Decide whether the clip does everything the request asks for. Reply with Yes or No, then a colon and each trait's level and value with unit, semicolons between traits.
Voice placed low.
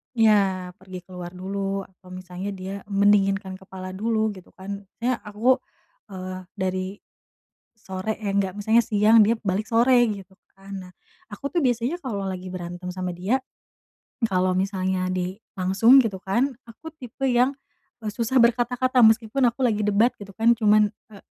No: high, 200 Hz